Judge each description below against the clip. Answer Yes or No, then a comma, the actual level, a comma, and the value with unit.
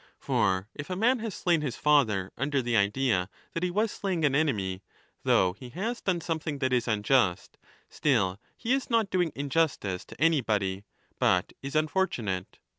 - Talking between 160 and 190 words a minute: Yes, average, 170 wpm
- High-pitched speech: No, medium, 140 Hz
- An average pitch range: No, wide, 9.0 semitones